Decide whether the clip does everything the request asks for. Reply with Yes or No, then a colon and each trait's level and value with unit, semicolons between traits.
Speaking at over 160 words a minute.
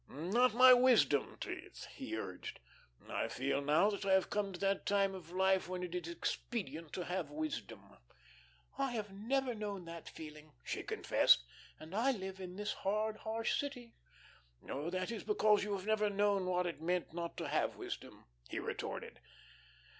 Yes: average, 175 wpm